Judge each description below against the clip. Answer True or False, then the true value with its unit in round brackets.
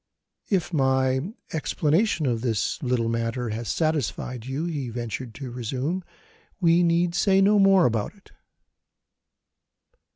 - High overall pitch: False (135 Hz)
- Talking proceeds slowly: True (125 wpm)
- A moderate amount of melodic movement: False (6.1 semitones)